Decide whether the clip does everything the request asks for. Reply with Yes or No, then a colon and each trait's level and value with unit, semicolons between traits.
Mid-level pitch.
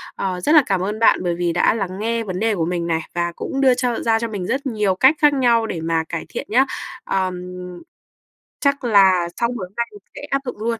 No: high, 215 Hz